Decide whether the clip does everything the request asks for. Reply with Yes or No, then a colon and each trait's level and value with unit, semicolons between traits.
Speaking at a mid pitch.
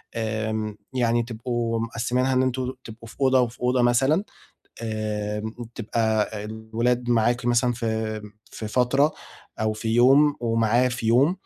No: low, 115 Hz